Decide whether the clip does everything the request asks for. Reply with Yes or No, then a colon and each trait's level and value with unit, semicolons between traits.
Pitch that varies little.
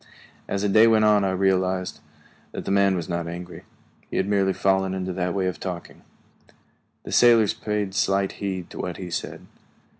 Yes: narrow, 1.5 semitones